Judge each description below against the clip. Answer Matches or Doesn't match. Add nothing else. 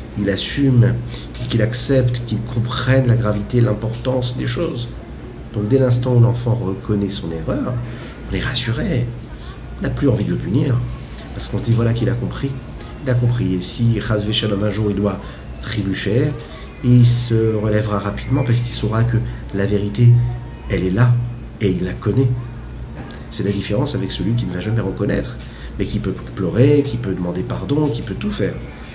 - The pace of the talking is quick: Doesn't match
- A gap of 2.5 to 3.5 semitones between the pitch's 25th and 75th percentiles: Matches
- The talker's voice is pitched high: Doesn't match